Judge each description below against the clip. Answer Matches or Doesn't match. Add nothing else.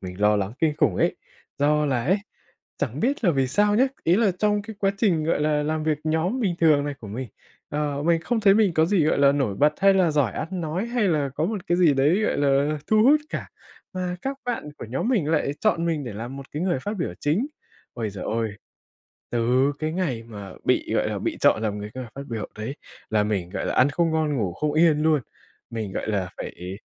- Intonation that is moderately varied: Doesn't match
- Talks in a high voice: Doesn't match